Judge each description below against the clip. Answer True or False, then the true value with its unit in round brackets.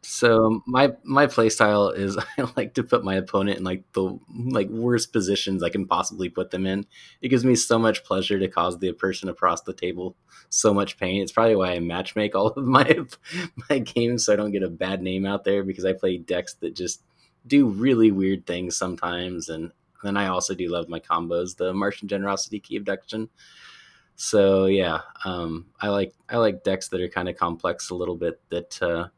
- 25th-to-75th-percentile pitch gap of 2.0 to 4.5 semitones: True (3.3 semitones)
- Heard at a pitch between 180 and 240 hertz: False (95 Hz)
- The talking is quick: True (210 wpm)